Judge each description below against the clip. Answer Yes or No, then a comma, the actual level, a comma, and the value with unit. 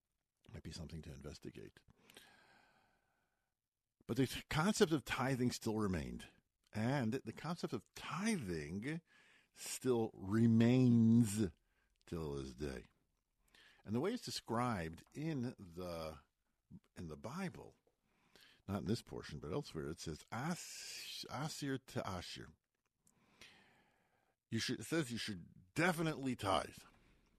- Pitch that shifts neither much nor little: No, wide, 7.6 semitones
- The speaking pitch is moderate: No, low, 115 Hz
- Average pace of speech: No, slow, 110 wpm